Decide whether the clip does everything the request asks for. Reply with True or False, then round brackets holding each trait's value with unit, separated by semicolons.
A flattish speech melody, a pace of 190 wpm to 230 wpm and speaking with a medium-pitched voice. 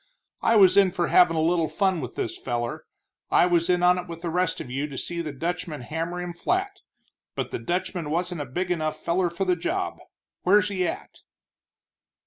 True (2.1 semitones; 205 wpm; 175 Hz)